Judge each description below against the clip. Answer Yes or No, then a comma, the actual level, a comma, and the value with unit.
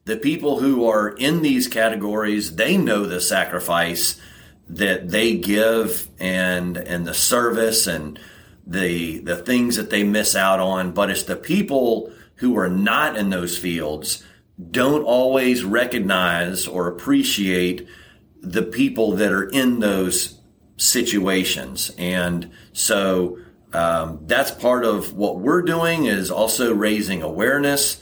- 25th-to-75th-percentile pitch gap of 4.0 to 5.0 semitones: Yes, average, 4.4 semitones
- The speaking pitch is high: No, low, 100 Hz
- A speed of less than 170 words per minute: Yes, slow, 135 wpm